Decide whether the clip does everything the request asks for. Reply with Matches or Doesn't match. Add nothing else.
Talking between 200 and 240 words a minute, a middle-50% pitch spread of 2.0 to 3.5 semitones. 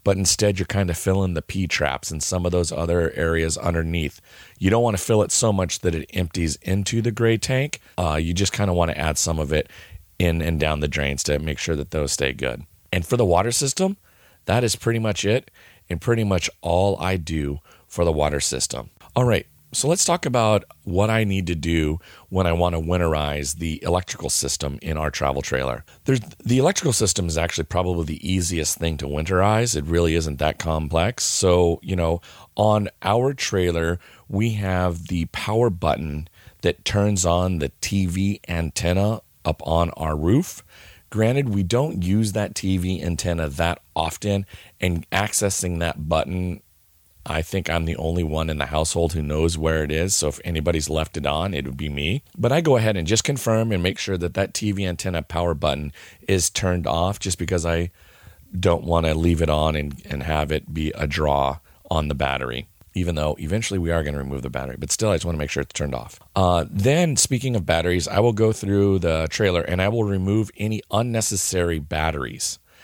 Doesn't match